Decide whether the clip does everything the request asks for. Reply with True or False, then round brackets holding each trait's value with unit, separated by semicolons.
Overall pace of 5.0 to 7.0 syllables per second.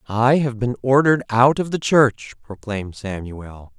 False (4.5 syllables/s)